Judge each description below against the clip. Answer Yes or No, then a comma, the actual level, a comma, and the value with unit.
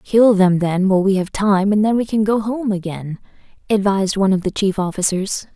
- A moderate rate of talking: No, fast, 215 wpm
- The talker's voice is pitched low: No, high, 200 Hz